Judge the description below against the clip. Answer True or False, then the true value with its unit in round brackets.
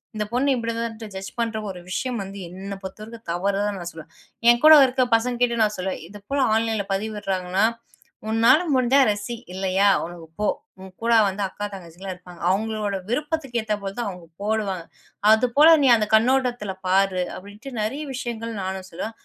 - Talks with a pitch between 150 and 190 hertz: False (210 Hz)